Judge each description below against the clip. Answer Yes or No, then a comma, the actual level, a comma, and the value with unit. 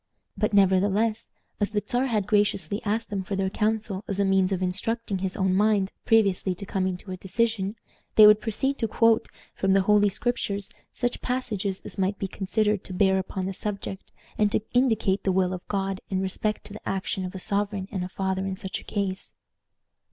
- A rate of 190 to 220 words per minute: Yes, average, 200 wpm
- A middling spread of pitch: No, narrow, 2.0 semitones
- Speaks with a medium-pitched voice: No, high, 200 Hz